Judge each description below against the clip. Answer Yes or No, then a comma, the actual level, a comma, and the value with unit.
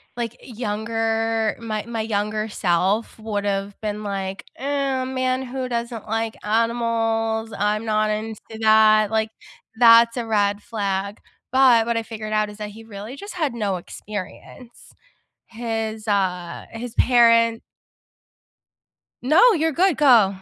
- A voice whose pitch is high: Yes, high, 225 Hz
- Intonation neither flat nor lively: No, narrow, 2.0 semitones